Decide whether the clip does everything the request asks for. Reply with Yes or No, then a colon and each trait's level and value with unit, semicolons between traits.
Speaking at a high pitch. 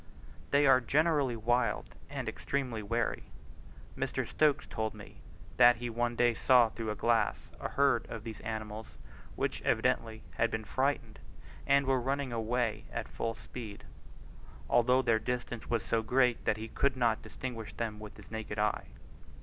No: low, 115 Hz